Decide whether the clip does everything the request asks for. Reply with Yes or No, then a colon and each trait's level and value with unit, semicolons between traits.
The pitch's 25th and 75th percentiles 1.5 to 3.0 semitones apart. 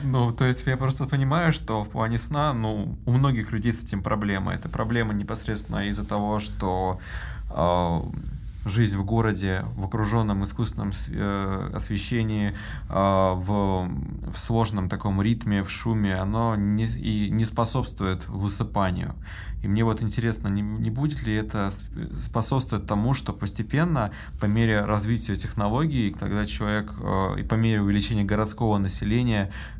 Yes: narrow, 2.5 semitones